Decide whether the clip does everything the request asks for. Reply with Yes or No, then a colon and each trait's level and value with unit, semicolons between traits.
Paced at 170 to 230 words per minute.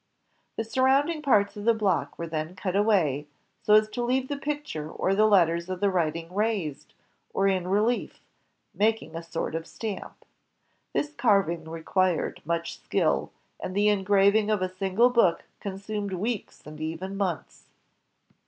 No: average, 155 wpm